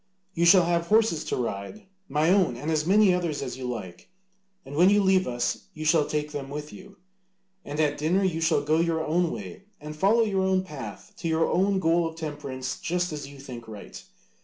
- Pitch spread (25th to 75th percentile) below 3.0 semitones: No, average, 4.0 semitones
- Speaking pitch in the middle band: Yes, medium, 160 Hz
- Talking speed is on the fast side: Yes, fast, 210 wpm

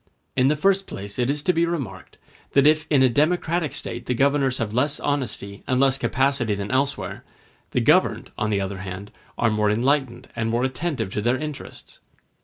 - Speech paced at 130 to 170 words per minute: No, average, 195 wpm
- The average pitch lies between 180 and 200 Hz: No, low, 130 Hz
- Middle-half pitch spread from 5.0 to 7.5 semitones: No, average, 4.6 semitones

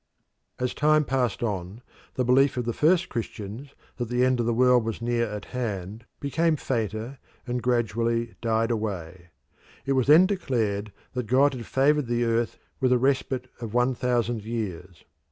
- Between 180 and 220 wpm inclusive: No, average, 170 wpm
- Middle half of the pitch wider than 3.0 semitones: No, average, 2.7 semitones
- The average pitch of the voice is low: Yes, low, 120 Hz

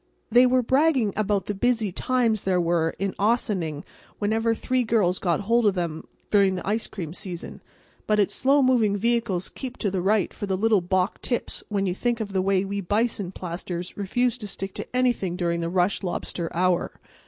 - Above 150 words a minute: Yes, average, 200 wpm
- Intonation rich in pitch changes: No, average, 4.0 semitones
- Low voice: No, high, 200 Hz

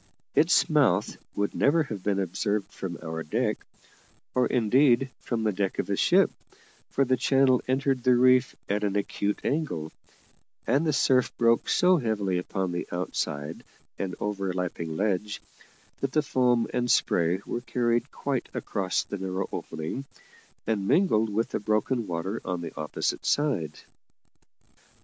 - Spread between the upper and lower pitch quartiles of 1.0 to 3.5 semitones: No, average, 5.3 semitones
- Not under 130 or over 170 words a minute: Yes, average, 150 wpm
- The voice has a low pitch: Yes, low, 105 Hz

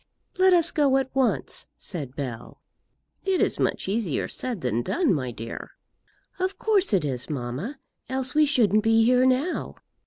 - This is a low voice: No, high, 235 Hz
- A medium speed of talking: Yes, average, 160 wpm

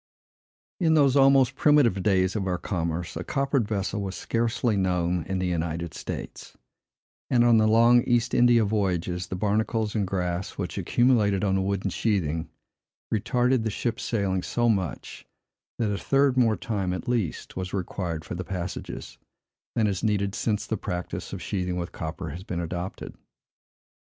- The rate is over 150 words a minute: Yes, average, 165 wpm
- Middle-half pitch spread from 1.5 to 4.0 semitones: No, average, 4.5 semitones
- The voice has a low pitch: Yes, low, 100 Hz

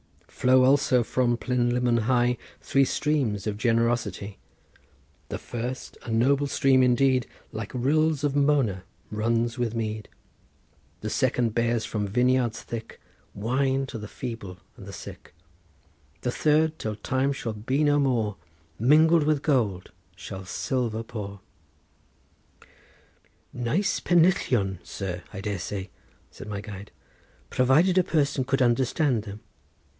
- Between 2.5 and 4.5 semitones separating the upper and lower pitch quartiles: Yes, average, 4.0 semitones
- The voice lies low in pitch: Yes, low, 120 Hz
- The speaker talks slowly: Yes, slow, 130 wpm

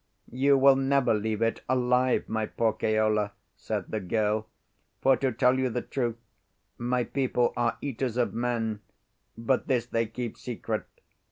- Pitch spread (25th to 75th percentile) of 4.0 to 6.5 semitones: No, average, 2.7 semitones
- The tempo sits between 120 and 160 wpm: Yes, average, 155 wpm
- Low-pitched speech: Yes, low, 120 Hz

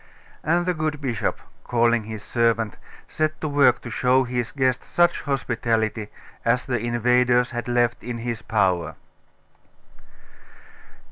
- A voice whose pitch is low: Yes, low, 120 Hz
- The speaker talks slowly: Yes, slow, 130 wpm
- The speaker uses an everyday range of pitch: No, narrow, 2.1 semitones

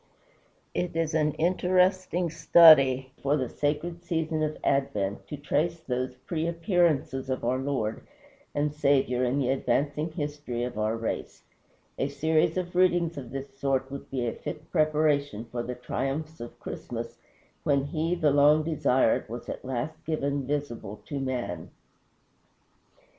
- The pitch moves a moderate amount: Yes, average, 3.6 semitones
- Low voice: No, medium, 145 Hz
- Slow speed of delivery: No, average, 150 wpm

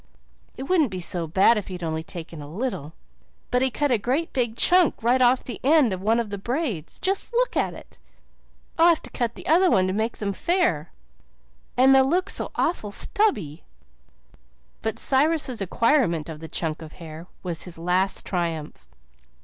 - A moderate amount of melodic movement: No, wide, 7.8 semitones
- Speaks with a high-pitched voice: Yes, high, 220 Hz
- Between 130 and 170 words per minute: No, average, 180 wpm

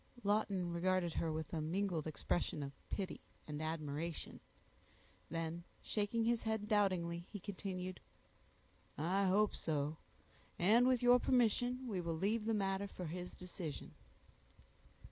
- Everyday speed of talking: No, slow, 130 wpm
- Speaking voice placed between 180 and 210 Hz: Yes, medium, 185 Hz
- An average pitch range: Yes, average, 4.1 semitones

